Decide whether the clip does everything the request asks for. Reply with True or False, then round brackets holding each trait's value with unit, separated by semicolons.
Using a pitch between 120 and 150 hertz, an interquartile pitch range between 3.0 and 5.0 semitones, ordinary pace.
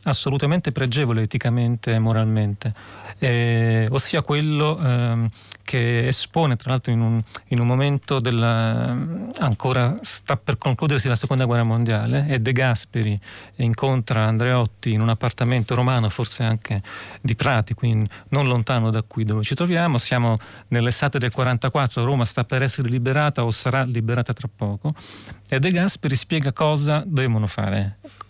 True (125 Hz; 3.3 semitones; 150 wpm)